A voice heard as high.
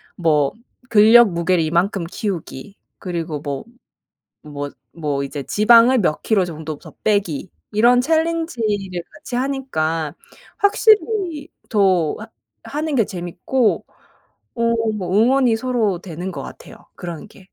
Yes: high, 200 Hz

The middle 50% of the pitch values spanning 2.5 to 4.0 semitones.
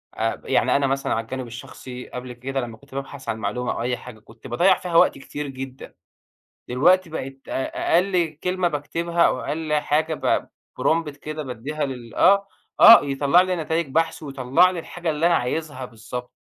No: average, 4.6 semitones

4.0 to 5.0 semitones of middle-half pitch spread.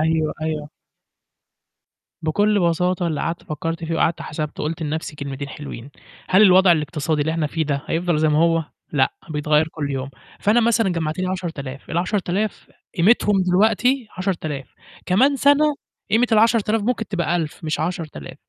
Yes: average, 4.4 semitones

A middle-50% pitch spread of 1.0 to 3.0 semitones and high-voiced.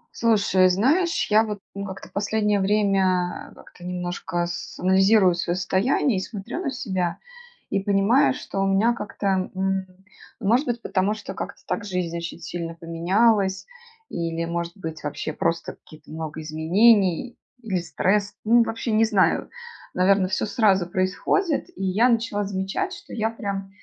No: average, 3.5 semitones; high, 195 Hz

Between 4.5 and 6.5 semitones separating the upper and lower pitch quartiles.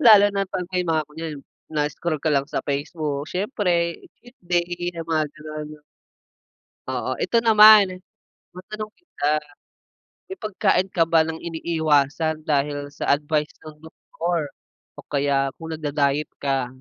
No: average, 3.5 semitones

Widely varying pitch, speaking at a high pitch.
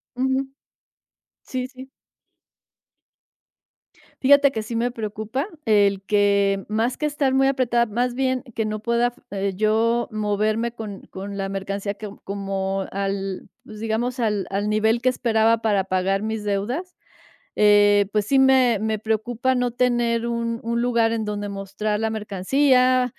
No: average, 3.2 semitones; high, 220 Hz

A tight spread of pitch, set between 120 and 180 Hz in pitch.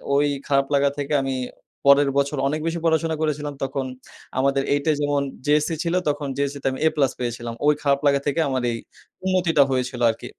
Yes: narrow, 1.6 semitones; medium, 140 Hz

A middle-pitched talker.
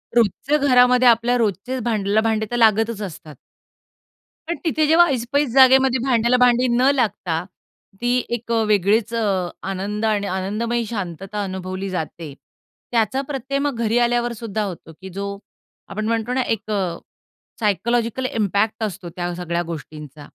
No: high, 220 Hz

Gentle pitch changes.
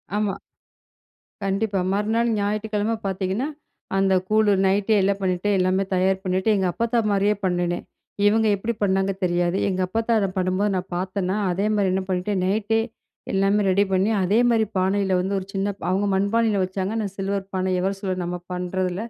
Yes: narrow, 1.8 semitones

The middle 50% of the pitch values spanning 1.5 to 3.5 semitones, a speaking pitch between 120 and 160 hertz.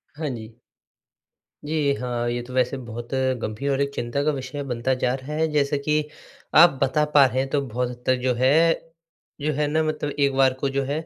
Yes: average, 2.7 semitones; low, 135 Hz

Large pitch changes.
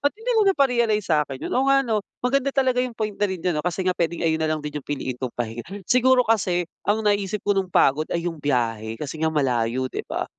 Yes: wide, 7.8 semitones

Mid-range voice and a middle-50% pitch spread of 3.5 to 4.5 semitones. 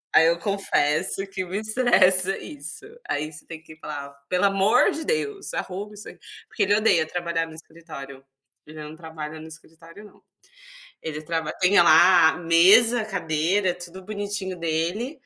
Yes: medium, 175 Hz; average, 4.2 semitones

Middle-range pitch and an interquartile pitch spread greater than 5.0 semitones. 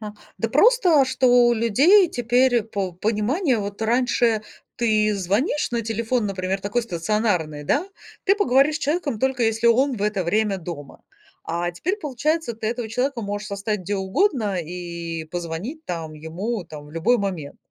No: high, 215 Hz; wide, 5.5 semitones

